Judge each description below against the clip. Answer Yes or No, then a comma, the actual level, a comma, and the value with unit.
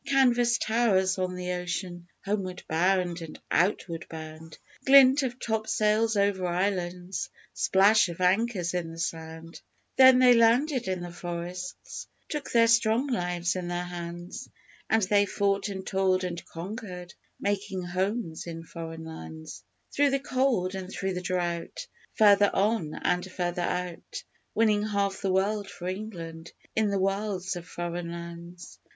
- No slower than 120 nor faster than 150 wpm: Yes, average, 145 wpm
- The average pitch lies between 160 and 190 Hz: Yes, medium, 185 Hz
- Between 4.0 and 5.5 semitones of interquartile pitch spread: No, average, 3.5 semitones